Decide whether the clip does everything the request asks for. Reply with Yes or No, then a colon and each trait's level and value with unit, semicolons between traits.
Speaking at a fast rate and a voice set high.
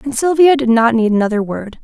Yes: fast, 230 wpm; high, 245 Hz